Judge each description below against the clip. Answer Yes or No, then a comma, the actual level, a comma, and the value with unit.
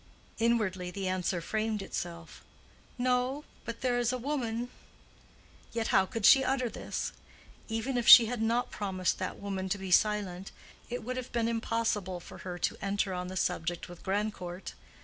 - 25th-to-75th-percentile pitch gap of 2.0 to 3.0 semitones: No, average, 4.2 semitones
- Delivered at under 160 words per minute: No, average, 170 wpm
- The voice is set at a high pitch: Yes, high, 215 Hz